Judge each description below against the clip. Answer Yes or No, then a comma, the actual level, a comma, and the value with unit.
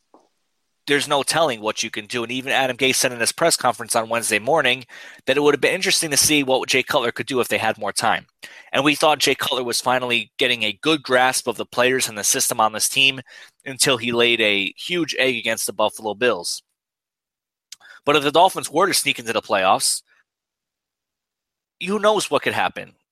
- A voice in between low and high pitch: No, low, 130 Hz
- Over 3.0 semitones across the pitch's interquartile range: Yes, average, 4.2 semitones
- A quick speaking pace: Yes, fast, 215 wpm